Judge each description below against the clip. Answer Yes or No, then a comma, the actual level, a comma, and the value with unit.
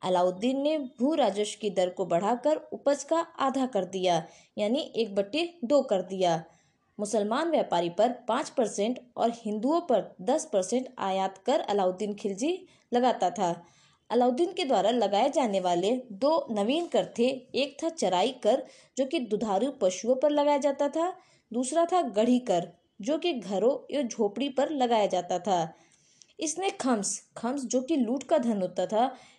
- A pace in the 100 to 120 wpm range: No, average, 165 wpm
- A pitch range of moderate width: No, wide, 6.7 semitones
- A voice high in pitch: Yes, high, 235 Hz